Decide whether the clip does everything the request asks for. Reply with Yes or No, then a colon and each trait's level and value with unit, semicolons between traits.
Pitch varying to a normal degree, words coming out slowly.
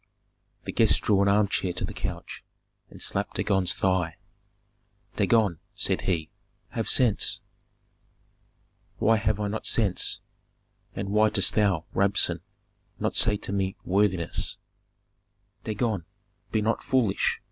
No: narrow, 2.3 semitones; slow, 125 wpm